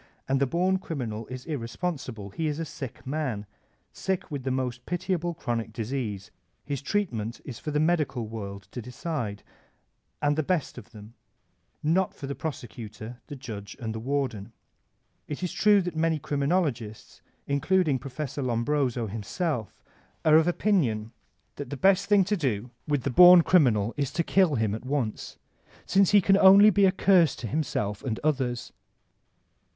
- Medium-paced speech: Yes, average, 165 wpm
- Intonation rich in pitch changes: Yes, wide, 6.4 semitones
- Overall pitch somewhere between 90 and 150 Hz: Yes, medium, 140 Hz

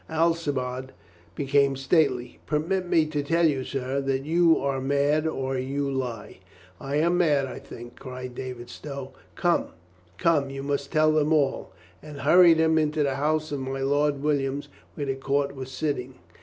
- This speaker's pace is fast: No, average, 170 wpm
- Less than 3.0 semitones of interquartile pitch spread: Yes, narrow, 2.5 semitones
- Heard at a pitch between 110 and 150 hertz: Yes, medium, 140 Hz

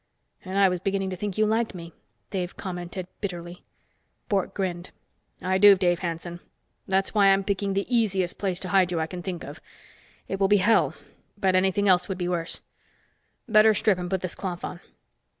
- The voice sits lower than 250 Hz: Yes, high, 190 Hz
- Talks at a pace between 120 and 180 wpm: No, average, 190 wpm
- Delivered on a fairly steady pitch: Yes, narrow, 1.9 semitones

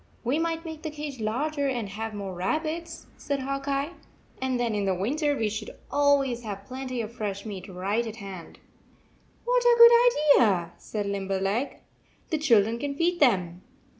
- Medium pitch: No, high, 245 Hz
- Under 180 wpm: Yes, average, 165 wpm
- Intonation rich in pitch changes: Yes, wide, 6.5 semitones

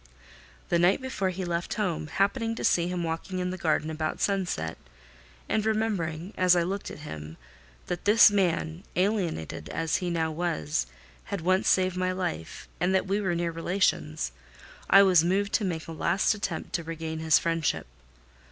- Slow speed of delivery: No, average, 175 wpm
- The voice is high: No, medium, 175 Hz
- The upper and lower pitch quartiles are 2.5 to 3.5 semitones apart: Yes, average, 3.1 semitones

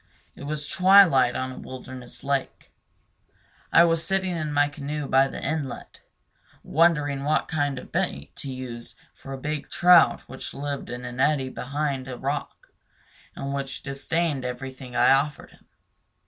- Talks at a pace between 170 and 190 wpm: No, average, 155 wpm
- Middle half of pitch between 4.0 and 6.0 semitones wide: No, average, 2.7 semitones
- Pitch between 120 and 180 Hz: Yes, medium, 140 Hz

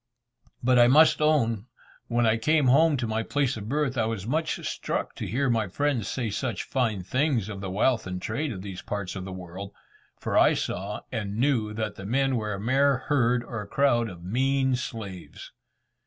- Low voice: Yes, low, 115 Hz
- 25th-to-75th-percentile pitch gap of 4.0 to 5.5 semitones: Yes, average, 4.6 semitones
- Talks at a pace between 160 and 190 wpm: No, average, 200 wpm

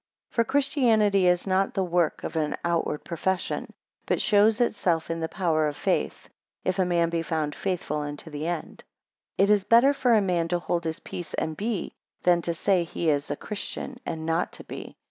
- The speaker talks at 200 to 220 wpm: Yes, fast, 205 wpm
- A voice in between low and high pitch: Yes, medium, 175 Hz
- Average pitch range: Yes, average, 3.8 semitones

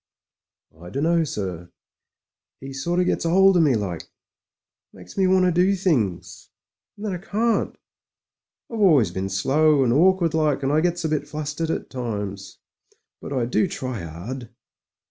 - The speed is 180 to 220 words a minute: No, average, 165 wpm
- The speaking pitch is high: No, medium, 150 Hz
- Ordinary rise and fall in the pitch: No, wide, 7.6 semitones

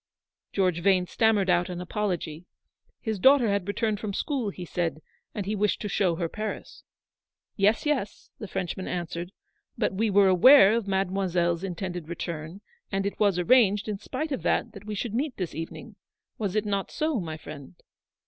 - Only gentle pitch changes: No, average, 3.3 semitones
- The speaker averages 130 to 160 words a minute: No, average, 175 wpm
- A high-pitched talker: Yes, high, 195 Hz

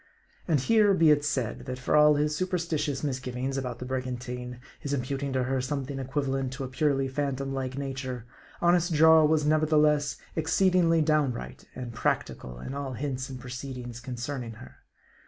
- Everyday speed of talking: Yes, average, 165 wpm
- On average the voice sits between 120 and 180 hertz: Yes, low, 135 Hz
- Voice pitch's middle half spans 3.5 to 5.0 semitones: No, average, 3.0 semitones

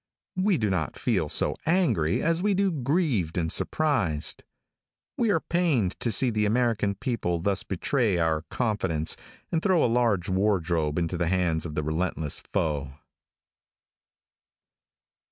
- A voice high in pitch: No, low, 100 Hz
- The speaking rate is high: No, average, 140 wpm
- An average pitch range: No, wide, 8.7 semitones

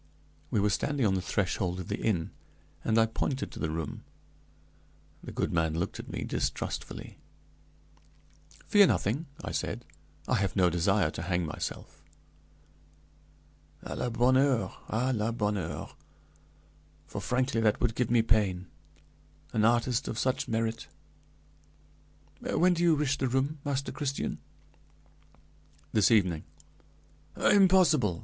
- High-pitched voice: No, low, 115 Hz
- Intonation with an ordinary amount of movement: No, wide, 5.8 semitones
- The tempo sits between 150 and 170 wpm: No, slow, 135 wpm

